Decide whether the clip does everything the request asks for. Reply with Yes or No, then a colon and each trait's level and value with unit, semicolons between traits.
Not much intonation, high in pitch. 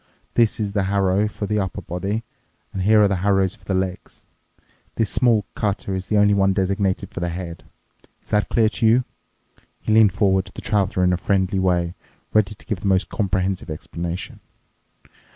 No: narrow, 2.1 semitones; very low, 95 Hz